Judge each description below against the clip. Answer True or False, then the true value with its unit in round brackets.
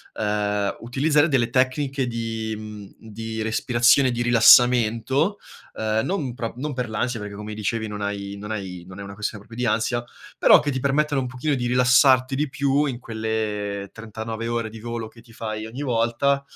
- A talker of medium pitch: False (115 Hz)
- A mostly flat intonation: False (3.0 semitones)